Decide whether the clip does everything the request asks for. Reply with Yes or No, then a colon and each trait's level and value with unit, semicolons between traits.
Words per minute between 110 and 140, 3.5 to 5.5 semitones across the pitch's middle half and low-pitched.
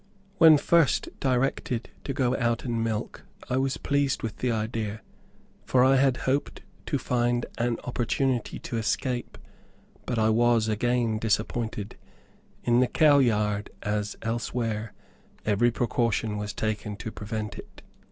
No: slow, 135 wpm; average, 2.7 semitones; low, 120 Hz